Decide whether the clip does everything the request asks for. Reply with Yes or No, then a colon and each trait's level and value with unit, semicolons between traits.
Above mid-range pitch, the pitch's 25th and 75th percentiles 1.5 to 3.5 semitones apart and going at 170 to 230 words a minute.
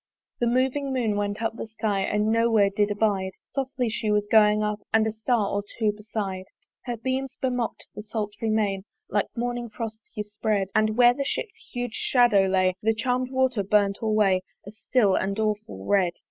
Yes: high, 215 Hz; average, 2.8 semitones; average, 185 wpm